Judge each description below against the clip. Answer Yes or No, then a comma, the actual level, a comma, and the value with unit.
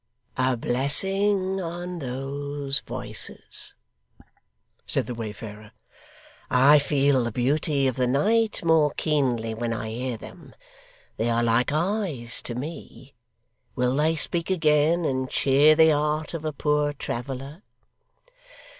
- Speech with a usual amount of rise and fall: Yes, average, 4.0 semitones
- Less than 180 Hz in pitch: Yes, medium, 140 Hz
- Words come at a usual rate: No, slow, 125 wpm